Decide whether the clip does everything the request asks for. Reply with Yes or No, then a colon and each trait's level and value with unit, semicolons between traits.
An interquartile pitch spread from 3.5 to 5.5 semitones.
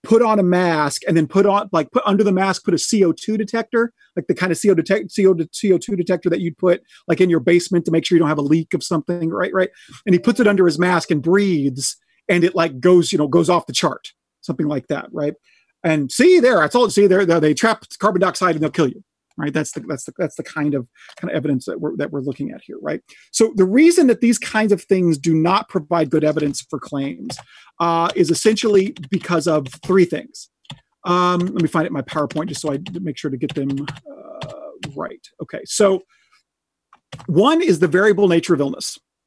Yes: average, 4.0 semitones